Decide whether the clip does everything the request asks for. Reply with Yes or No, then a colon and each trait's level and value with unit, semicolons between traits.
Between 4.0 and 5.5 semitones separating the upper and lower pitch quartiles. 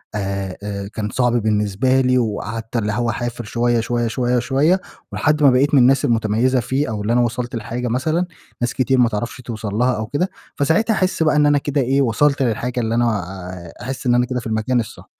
No: average, 3.2 semitones